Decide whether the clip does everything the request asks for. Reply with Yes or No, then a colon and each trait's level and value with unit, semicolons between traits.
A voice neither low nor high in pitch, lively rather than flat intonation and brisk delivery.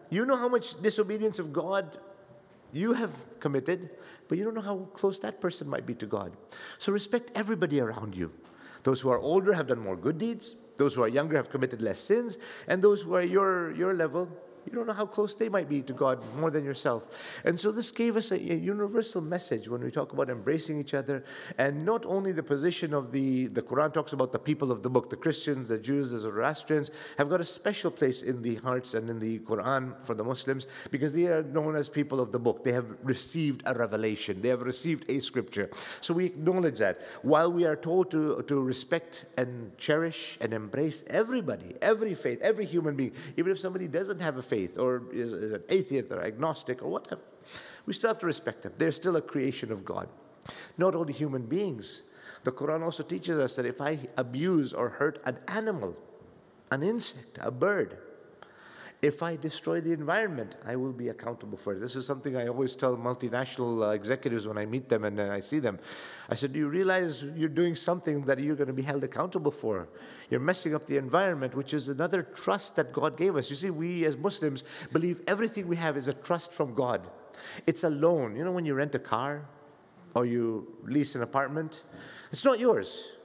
Yes: medium, 150 Hz; wide, 5.7 semitones; fast, 210 wpm